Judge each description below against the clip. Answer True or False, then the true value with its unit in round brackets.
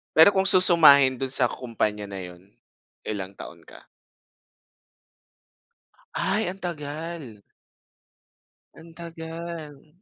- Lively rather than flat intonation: True (6.6 semitones)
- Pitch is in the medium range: True (150 Hz)